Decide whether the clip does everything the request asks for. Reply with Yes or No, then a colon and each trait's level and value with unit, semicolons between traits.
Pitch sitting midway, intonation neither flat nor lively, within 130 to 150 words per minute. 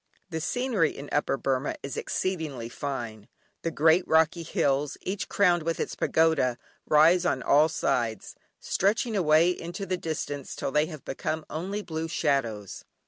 Yes: medium, 160 Hz; average, 4.0 semitones; average, 145 wpm